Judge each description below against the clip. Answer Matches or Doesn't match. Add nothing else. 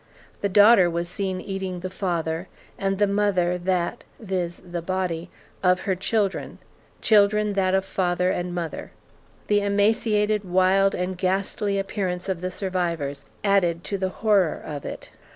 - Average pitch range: Doesn't match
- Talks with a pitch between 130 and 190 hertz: Matches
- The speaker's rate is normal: Matches